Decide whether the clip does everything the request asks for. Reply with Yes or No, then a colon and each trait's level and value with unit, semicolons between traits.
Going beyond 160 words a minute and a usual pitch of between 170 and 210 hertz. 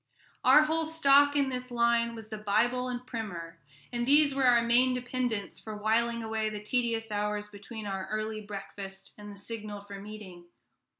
No: average, 175 wpm; high, 225 Hz